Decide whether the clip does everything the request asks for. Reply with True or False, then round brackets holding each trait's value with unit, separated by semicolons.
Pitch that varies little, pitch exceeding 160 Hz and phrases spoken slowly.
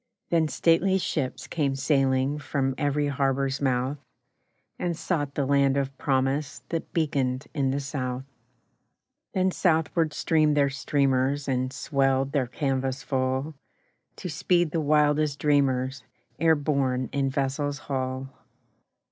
False (2.1 semitones; 140 Hz; 125 wpm)